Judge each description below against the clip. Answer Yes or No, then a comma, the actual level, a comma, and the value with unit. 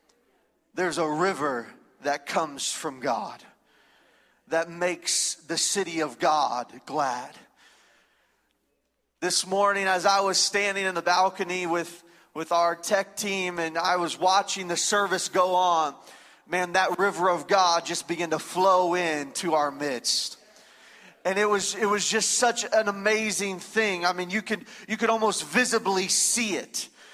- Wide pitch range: No, average, 2.8 semitones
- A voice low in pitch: No, medium, 185 Hz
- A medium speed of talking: Yes, average, 150 wpm